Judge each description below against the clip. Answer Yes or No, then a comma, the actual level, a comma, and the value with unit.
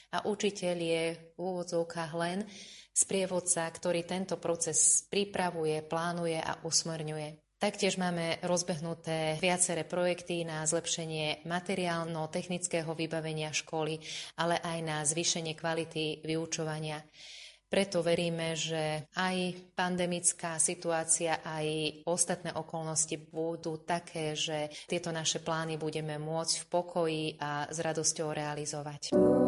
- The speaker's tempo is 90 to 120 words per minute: Yes, slow, 110 wpm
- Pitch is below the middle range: No, medium, 165 Hz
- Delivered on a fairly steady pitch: Yes, narrow, 1.9 semitones